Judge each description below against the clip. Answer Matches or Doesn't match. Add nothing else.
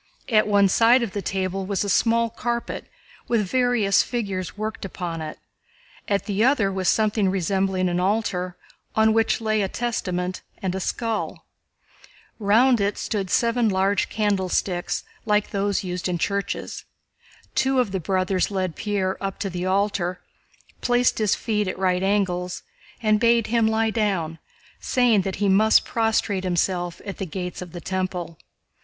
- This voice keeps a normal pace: Matches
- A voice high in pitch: Matches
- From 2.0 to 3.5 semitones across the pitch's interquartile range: Matches